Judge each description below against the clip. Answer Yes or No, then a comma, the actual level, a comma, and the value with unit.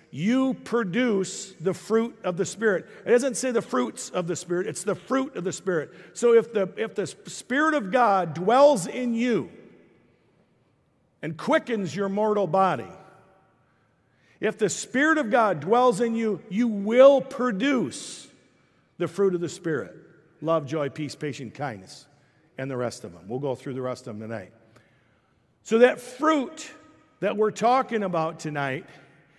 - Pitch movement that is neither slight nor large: No, wide, 7.8 semitones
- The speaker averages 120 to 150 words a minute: No, average, 160 wpm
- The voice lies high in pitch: Yes, high, 195 Hz